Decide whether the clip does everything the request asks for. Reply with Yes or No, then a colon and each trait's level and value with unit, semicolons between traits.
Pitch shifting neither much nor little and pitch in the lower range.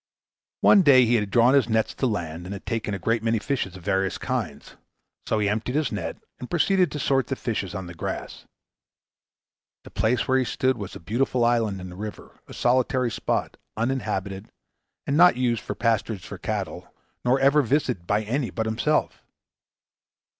Yes: average, 4.2 semitones; low, 115 Hz